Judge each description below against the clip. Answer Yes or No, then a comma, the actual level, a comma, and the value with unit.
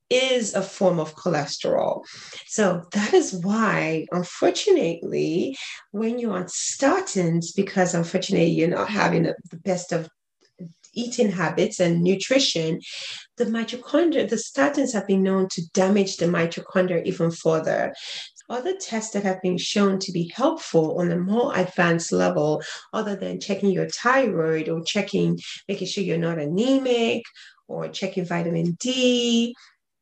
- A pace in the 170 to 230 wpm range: No, average, 140 wpm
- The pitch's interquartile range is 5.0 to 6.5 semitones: Yes, average, 5.3 semitones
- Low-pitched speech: No, high, 190 Hz